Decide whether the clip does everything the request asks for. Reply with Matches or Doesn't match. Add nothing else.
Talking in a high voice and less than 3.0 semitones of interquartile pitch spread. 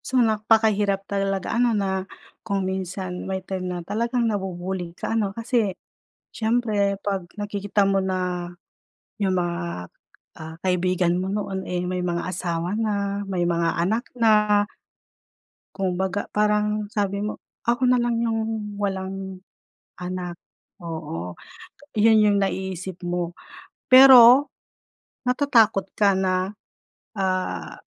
Matches